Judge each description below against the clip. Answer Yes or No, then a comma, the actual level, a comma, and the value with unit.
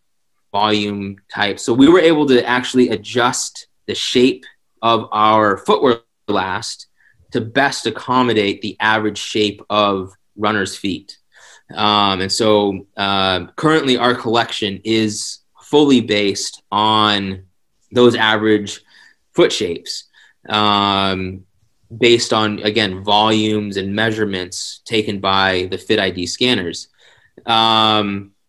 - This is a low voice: Yes, low, 105 Hz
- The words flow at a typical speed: No, slow, 110 wpm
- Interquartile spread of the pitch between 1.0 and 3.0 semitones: Yes, narrow, 2.6 semitones